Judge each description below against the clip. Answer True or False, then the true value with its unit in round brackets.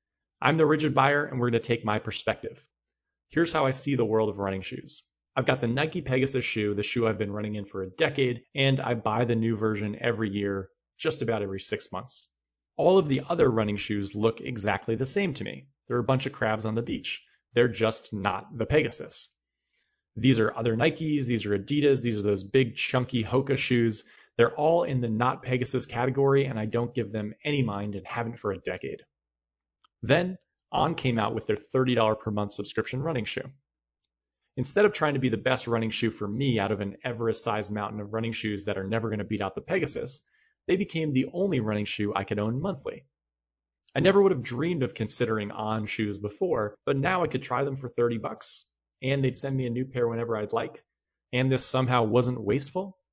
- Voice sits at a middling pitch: False (115 Hz)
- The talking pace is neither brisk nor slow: False (215 wpm)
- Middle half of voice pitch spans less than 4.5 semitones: True (4.0 semitones)